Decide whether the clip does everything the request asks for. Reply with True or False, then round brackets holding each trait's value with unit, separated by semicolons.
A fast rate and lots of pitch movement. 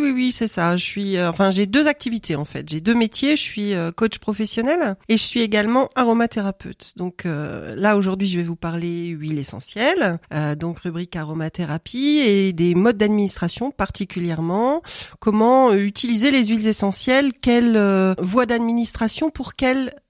False (160 wpm; 5.7 semitones)